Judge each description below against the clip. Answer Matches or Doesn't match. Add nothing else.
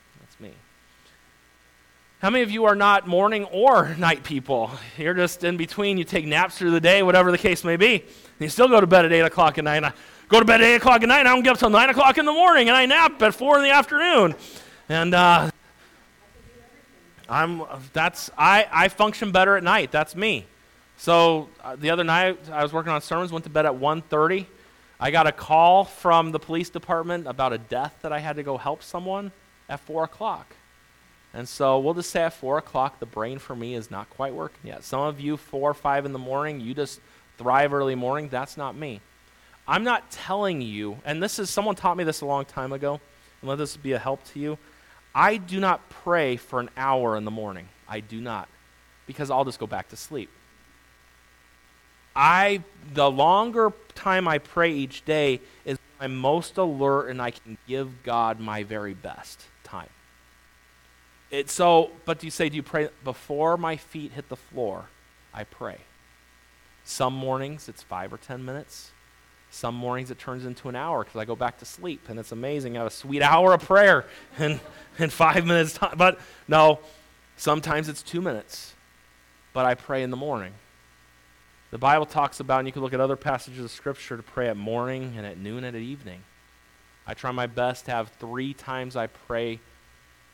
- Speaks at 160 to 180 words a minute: Doesn't match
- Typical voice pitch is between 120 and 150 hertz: Matches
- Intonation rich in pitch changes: Matches